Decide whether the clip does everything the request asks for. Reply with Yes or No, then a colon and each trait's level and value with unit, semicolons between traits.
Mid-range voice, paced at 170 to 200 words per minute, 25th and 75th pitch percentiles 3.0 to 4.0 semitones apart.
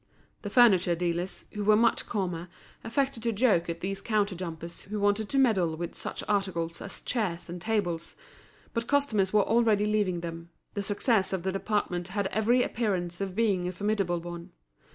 No: high, 195 Hz; average, 175 wpm; average, 3.7 semitones